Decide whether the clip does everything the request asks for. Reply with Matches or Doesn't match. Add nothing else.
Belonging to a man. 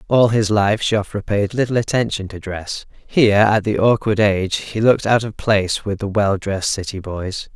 Matches